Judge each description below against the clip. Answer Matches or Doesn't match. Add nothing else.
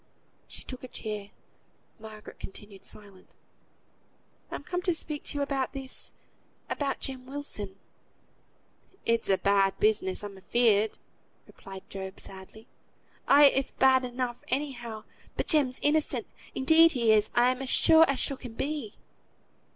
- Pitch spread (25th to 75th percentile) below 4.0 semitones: Doesn't match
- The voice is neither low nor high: Doesn't match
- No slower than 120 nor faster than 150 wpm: Matches